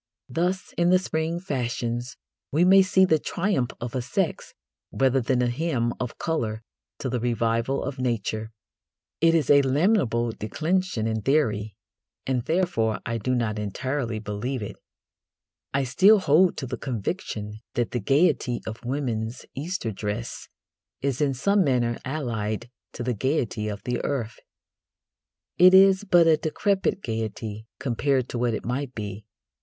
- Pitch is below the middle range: Yes, low, 125 Hz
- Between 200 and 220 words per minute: No, average, 150 wpm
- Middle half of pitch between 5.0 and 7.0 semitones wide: Yes, wide, 5.6 semitones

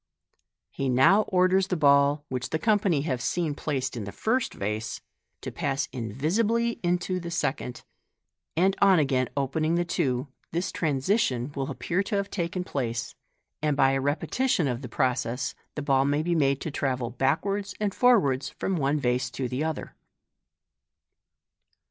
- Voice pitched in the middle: Yes, medium, 145 Hz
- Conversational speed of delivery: Yes, average, 160 wpm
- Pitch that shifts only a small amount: No, wide, 5.6 semitones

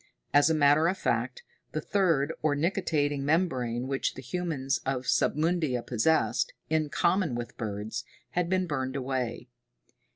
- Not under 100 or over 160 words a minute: Yes, average, 140 wpm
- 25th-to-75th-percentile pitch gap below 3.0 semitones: No, average, 4.3 semitones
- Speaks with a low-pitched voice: No, medium, 145 Hz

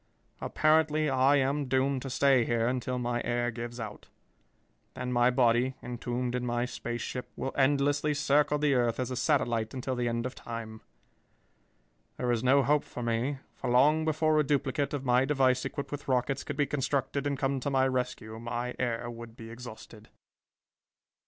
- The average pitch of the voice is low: Yes, low, 130 Hz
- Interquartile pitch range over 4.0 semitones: No, average, 2.7 semitones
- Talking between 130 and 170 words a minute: No, average, 180 wpm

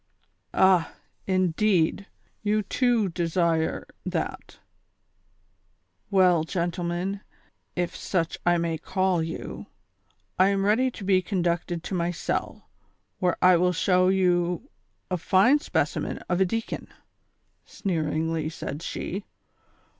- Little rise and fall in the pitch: Yes, narrow, 2.3 semitones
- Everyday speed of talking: No, slow, 110 wpm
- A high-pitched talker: No, medium, 180 Hz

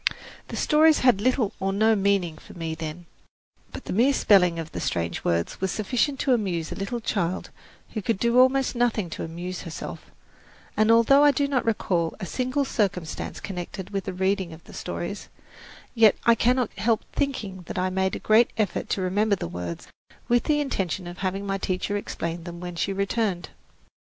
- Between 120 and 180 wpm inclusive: No, average, 190 wpm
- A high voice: Yes, high, 195 Hz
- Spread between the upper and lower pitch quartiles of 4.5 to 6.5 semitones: Yes, average, 4.9 semitones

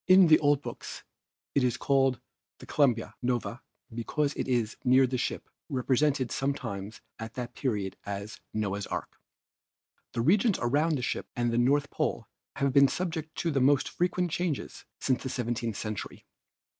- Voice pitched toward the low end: Yes, low, 130 Hz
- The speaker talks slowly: No, average, 155 wpm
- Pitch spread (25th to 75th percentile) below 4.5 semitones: Yes, average, 3.7 semitones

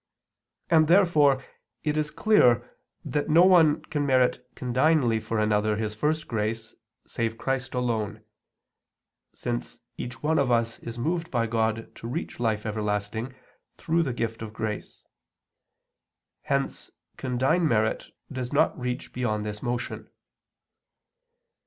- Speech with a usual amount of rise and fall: Yes, average, 5.0 semitones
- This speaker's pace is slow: Yes, slow, 125 wpm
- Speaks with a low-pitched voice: Yes, low, 125 Hz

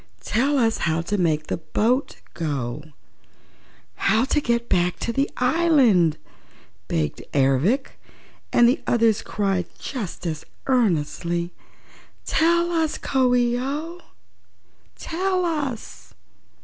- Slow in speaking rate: Yes, slow, 110 wpm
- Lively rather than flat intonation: Yes, wide, 8.2 semitones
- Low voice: No, high, 235 Hz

